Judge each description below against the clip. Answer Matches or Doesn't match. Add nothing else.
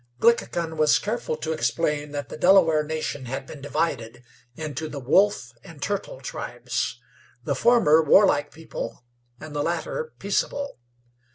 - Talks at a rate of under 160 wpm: Matches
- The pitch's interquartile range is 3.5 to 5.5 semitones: Matches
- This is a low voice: Doesn't match